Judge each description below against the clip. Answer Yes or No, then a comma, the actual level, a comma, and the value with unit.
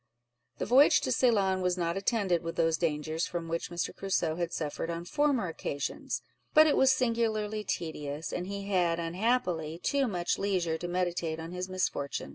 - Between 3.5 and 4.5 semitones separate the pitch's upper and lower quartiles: Yes, average, 4.0 semitones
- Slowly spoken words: No, average, 175 wpm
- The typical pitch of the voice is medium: Yes, medium, 180 Hz